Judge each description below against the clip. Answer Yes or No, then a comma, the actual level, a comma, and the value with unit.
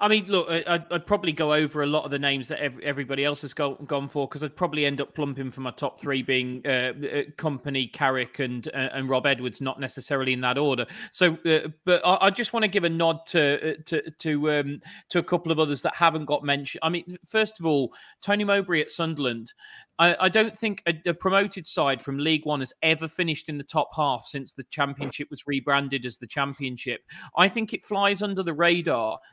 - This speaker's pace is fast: Yes, fast, 225 wpm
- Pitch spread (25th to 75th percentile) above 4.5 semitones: No, average, 3.8 semitones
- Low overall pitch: No, medium, 150 Hz